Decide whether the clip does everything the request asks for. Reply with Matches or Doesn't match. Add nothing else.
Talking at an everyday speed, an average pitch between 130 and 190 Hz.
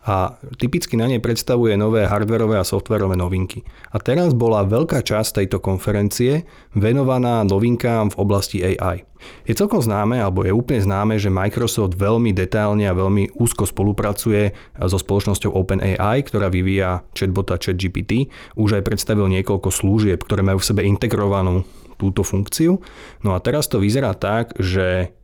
Doesn't match